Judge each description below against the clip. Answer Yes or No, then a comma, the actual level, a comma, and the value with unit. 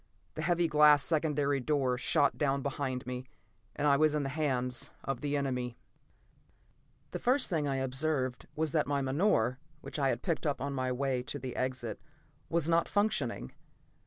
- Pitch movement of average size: Yes, average, 3.0 semitones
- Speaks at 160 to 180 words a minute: Yes, average, 175 wpm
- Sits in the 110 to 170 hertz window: Yes, medium, 140 Hz